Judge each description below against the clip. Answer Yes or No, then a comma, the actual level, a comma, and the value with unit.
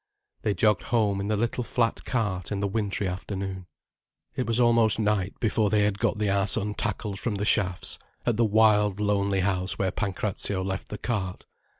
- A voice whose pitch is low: Yes, low, 105 Hz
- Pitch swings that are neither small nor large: No, narrow, 2.1 semitones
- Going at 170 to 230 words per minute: Yes, average, 185 wpm